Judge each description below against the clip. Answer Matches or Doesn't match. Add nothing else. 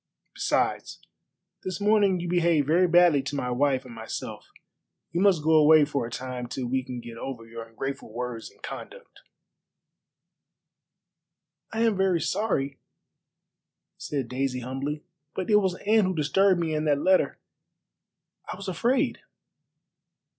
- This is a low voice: Doesn't match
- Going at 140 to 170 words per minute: Matches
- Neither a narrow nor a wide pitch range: Doesn't match